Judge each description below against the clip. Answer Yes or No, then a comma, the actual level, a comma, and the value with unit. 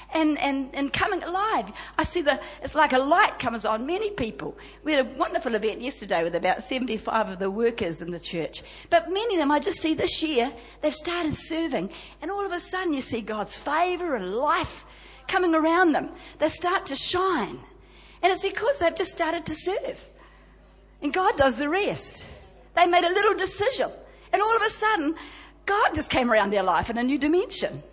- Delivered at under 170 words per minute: No, fast, 205 wpm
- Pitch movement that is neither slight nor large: No, wide, 6.2 semitones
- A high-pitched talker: Yes, very high, 325 Hz